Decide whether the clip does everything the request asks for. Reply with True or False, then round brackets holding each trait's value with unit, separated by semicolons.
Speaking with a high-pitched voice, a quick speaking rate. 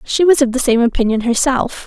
True (250 Hz; 225 wpm)